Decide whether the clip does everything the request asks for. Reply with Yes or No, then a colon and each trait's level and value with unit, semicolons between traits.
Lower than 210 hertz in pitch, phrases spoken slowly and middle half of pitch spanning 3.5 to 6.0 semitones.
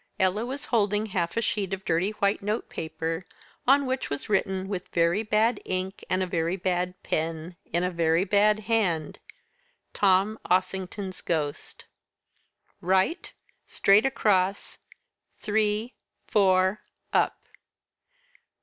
No: high, 190 Hz; slow, 120 wpm; average, 2.9 semitones